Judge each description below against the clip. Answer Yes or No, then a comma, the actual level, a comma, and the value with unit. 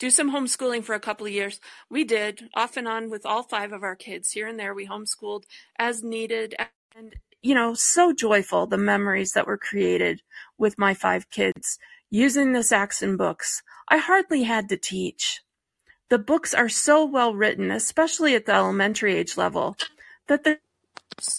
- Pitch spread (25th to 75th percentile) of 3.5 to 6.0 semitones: Yes, average, 5.1 semitones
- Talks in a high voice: Yes, high, 230 Hz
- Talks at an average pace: Yes, average, 175 wpm